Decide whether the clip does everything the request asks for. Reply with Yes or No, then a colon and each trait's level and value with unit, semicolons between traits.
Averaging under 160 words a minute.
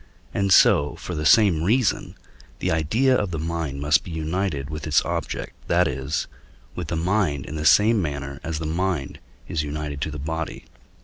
No: average, 185 wpm